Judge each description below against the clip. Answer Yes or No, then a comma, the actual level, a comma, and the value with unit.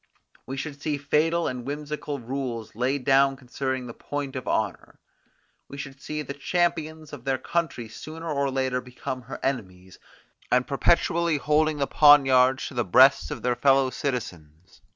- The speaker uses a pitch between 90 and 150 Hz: Yes, low, 135 Hz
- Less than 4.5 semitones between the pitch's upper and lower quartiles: Yes, average, 2.7 semitones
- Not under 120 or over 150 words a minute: No, average, 160 wpm